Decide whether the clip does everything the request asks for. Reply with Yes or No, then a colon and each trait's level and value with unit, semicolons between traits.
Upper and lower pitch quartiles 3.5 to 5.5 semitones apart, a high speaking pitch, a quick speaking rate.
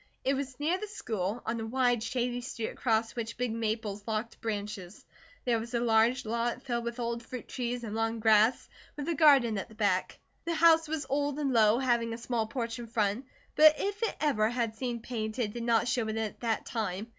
No: narrow, 2.5 semitones; high, 235 Hz; fast, 215 wpm